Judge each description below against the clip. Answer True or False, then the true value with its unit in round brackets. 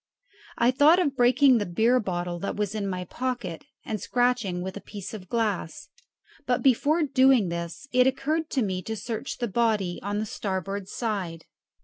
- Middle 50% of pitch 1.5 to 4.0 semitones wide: False (5.1 semitones)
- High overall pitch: True (220 Hz)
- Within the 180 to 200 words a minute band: True (185 wpm)